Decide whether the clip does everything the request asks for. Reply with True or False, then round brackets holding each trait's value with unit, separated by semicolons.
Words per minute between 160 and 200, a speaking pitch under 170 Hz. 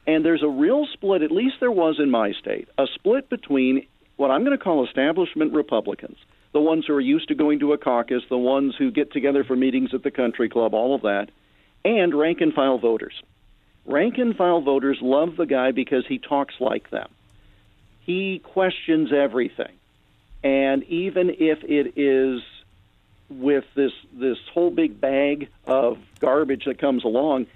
True (180 wpm; 140 Hz)